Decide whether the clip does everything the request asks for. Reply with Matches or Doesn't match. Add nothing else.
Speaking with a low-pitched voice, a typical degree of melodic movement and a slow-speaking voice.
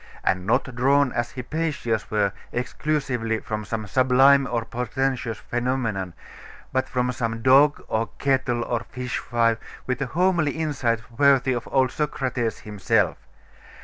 Matches